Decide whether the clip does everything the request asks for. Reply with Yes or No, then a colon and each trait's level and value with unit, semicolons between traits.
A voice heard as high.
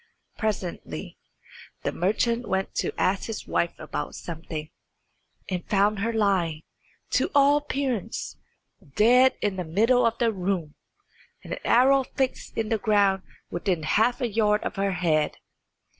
Yes: high, 205 Hz